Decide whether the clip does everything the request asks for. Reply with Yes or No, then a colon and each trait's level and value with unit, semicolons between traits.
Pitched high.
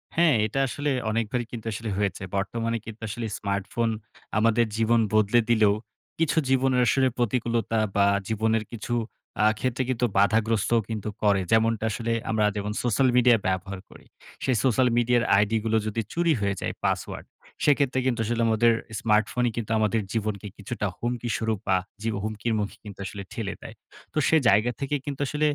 No: low, 115 Hz